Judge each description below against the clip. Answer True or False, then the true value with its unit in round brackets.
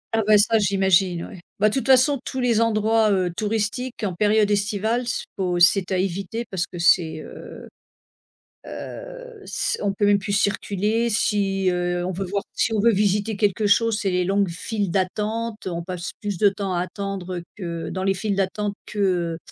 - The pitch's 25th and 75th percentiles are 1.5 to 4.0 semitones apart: True (2.8 semitones)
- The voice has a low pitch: False (200 Hz)